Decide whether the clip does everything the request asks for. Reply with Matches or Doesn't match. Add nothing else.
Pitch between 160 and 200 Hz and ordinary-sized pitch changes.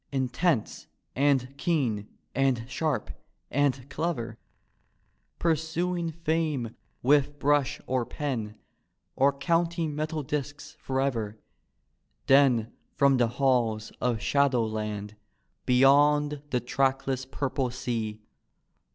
Doesn't match